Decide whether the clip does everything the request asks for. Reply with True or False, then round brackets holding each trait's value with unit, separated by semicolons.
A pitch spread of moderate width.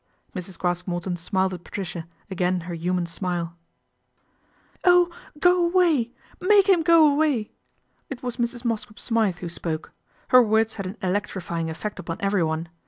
False (6.3 semitones)